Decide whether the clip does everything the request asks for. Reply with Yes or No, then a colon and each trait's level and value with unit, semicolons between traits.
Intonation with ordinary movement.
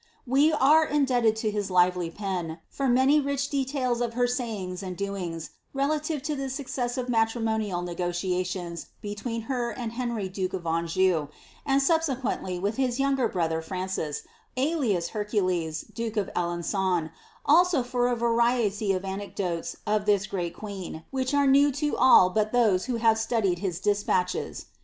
No: wide, 5.8 semitones